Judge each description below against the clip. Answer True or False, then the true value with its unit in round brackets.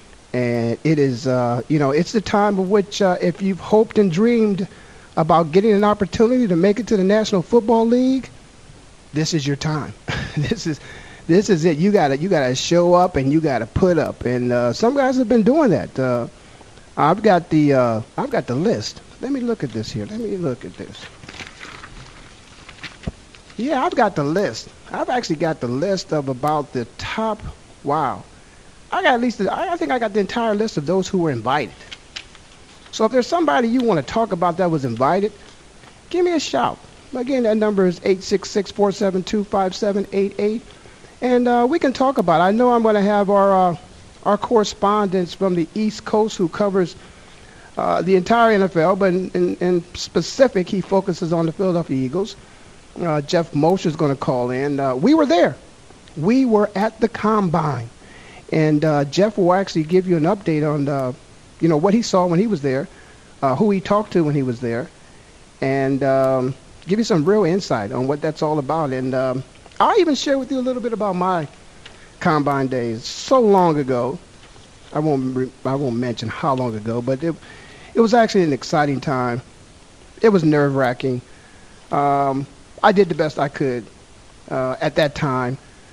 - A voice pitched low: False (180 Hz)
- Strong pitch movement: True (7.0 semitones)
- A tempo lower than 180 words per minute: False (190 wpm)